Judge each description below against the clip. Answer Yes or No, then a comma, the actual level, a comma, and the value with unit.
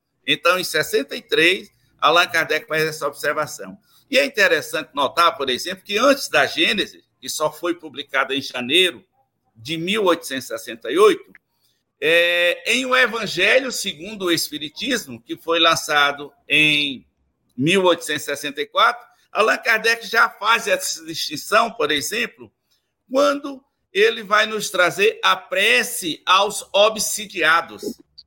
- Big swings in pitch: Yes, wide, 8.3 semitones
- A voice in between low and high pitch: Yes, medium, 180 Hz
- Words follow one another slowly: Yes, slow, 115 wpm